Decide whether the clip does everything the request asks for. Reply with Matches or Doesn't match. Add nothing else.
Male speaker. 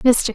Doesn't match